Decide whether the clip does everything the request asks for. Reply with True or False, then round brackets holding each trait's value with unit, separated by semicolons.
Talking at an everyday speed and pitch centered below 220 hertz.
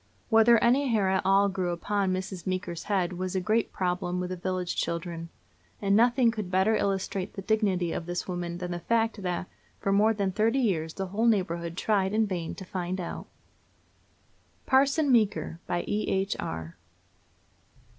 True (170 wpm; 190 Hz)